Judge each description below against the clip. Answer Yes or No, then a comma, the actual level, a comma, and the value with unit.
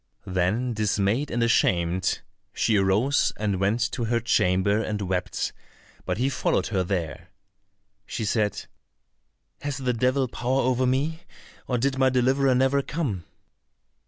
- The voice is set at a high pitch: No, low, 115 Hz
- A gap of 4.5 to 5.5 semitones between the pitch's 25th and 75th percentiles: Yes, average, 5.0 semitones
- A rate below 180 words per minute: Yes, slow, 135 wpm